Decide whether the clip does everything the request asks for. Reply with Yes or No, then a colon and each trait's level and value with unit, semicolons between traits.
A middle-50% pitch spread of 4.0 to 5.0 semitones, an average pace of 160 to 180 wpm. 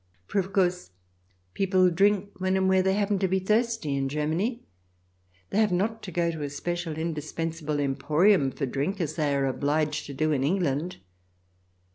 Yes: average, 4.3 semitones; average, 175 wpm